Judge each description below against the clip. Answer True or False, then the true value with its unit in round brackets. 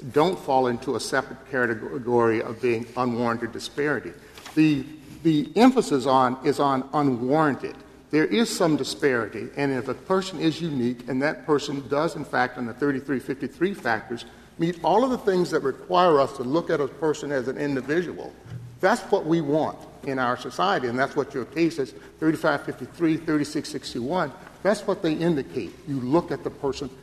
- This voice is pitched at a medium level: True (145 Hz)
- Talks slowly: False (170 wpm)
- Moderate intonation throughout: True (4.1 semitones)